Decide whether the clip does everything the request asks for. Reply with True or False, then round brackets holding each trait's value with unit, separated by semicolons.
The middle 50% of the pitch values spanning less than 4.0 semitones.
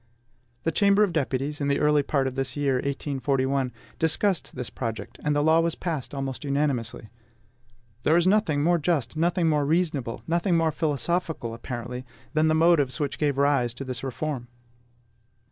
True (3.6 semitones)